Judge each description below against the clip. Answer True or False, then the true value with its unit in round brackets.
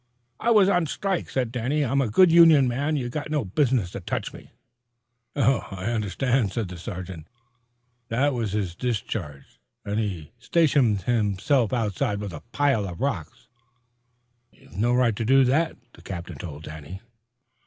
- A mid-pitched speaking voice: False (120 Hz)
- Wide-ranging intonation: True (6.1 semitones)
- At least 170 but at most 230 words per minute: False (160 wpm)